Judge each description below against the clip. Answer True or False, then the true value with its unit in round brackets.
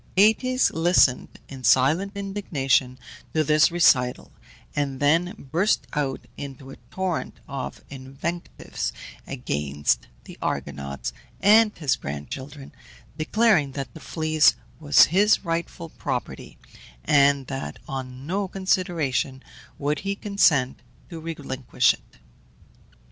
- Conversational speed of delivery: False (110 wpm)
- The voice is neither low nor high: True (150 Hz)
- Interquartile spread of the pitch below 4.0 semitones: False (5.0 semitones)